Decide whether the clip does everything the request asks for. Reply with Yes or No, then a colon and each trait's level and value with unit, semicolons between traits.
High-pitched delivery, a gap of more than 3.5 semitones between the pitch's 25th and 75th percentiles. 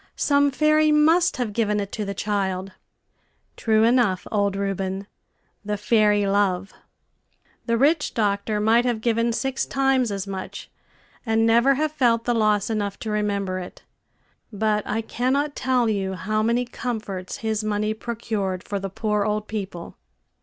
No: high, 215 Hz; average, 3.1 semitones